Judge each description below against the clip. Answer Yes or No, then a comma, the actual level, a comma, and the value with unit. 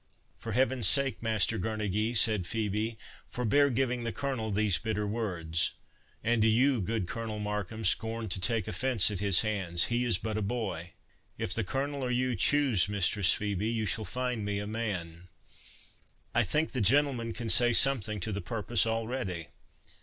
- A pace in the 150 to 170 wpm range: Yes, average, 165 wpm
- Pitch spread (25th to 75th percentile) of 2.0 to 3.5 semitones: Yes, average, 3.0 semitones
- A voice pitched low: Yes, low, 110 Hz